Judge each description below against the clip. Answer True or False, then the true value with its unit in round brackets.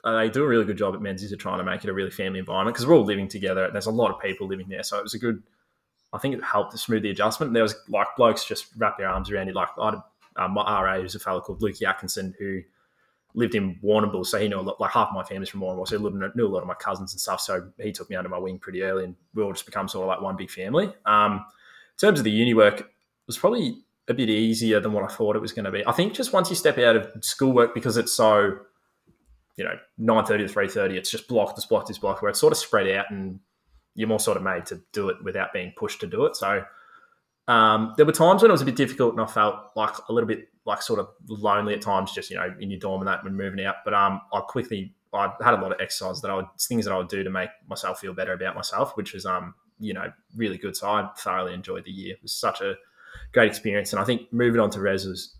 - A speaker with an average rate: False (295 wpm)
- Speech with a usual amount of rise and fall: True (3.4 semitones)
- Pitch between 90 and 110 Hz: True (105 Hz)